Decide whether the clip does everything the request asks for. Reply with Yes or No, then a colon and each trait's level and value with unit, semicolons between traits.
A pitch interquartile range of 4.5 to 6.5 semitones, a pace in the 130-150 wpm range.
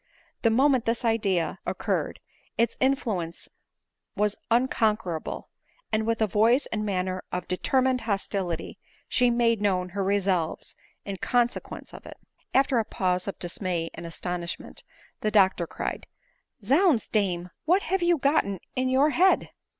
Yes: average, 5.3 semitones; average, 140 wpm